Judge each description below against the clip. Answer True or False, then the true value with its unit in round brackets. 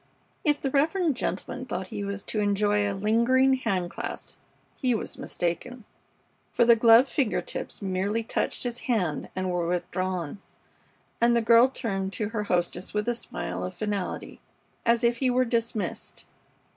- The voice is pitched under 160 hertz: False (215 Hz)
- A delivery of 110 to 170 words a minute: True (160 wpm)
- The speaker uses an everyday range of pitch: True (4.1 semitones)